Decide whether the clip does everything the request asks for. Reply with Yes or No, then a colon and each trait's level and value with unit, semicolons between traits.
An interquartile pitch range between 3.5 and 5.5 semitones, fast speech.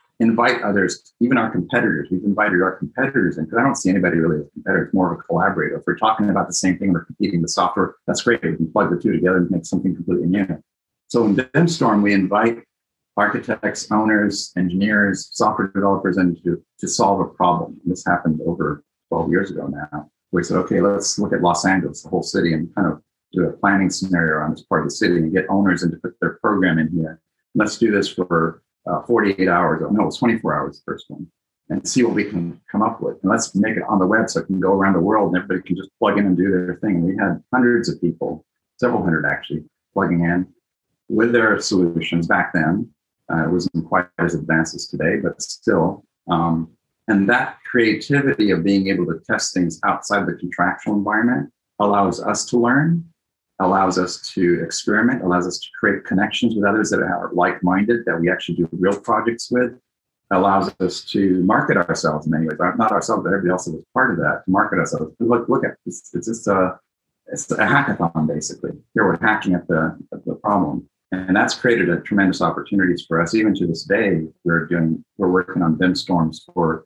No: average, 3.1 semitones; fast, 210 wpm